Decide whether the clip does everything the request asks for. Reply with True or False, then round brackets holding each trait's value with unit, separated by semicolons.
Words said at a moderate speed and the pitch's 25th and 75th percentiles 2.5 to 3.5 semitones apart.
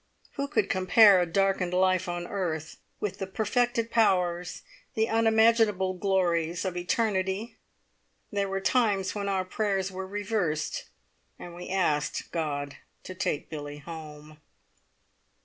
False (130 wpm; 3.1 semitones)